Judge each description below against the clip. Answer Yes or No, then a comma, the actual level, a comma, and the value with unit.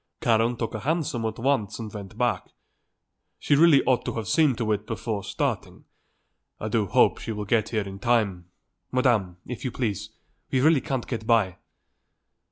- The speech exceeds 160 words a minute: Yes, average, 180 wpm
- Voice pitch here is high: No, low, 115 Hz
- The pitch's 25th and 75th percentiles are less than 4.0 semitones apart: Yes, average, 3.3 semitones